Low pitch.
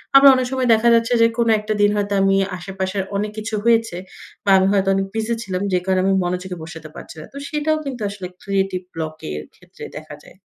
No: high, 200 Hz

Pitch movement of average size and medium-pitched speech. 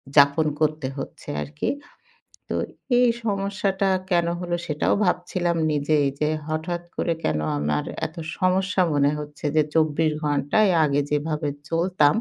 Yes: average, 3.6 semitones; medium, 155 Hz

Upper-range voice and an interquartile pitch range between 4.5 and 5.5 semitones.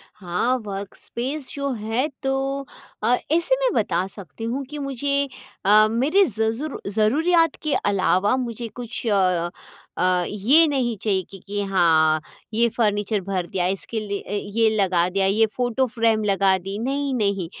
Yes: high, 220 Hz; average, 5.1 semitones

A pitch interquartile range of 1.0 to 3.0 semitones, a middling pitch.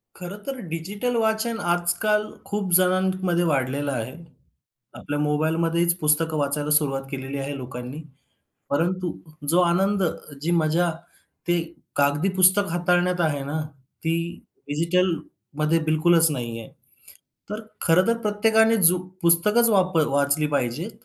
No: average, 4.0 semitones; medium, 170 Hz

